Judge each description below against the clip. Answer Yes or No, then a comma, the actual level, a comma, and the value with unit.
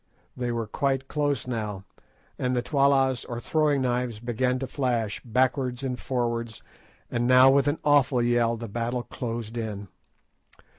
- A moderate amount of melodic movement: No, narrow, 2.2 semitones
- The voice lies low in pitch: Yes, low, 125 Hz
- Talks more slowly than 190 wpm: Yes, average, 150 wpm